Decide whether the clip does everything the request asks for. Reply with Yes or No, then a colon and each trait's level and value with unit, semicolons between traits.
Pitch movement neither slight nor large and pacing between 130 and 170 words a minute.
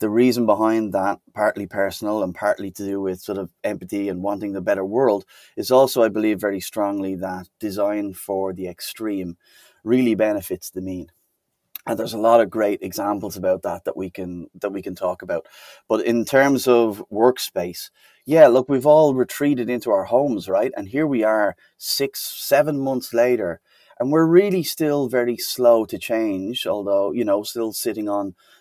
No: average, 3.9 semitones; average, 180 wpm